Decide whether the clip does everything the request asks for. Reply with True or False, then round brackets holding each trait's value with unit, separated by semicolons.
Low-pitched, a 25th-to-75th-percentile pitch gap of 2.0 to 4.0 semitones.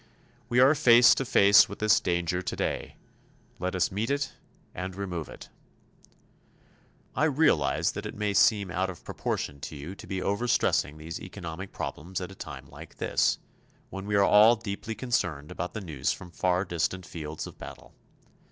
True (95 Hz; 3.7 semitones)